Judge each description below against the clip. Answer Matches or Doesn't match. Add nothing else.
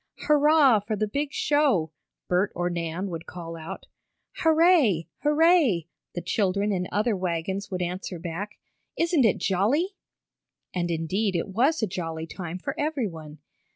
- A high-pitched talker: Matches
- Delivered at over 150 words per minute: Doesn't match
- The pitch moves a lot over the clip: Matches